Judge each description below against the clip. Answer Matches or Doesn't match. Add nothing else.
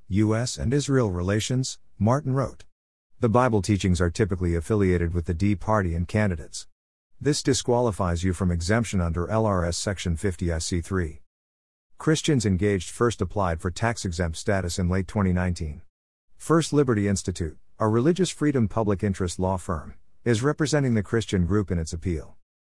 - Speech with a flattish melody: Doesn't match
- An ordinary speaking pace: Matches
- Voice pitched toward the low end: Matches